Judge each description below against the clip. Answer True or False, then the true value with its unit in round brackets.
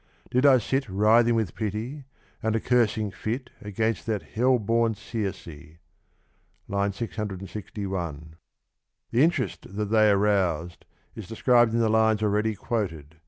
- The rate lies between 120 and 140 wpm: True (135 wpm)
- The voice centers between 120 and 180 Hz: False (110 Hz)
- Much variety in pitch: False (2.9 semitones)